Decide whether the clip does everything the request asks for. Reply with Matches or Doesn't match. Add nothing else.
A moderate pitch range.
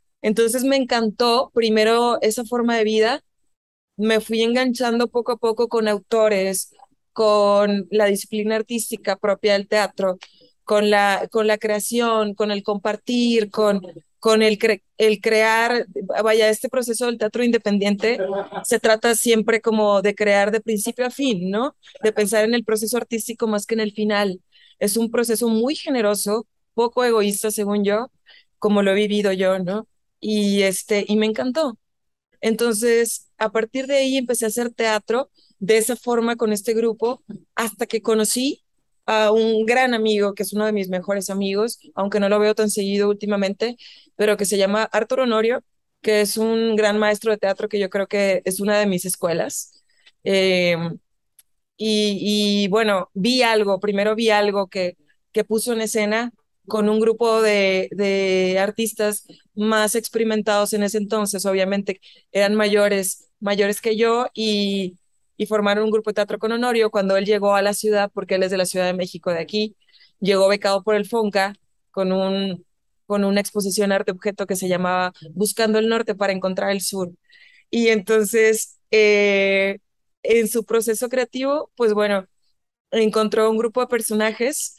Doesn't match